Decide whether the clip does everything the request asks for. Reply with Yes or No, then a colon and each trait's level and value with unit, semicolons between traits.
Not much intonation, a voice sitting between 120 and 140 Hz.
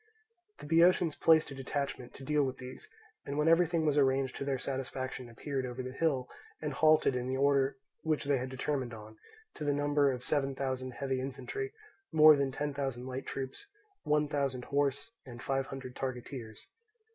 Yes: narrow, 2.2 semitones; low, 135 Hz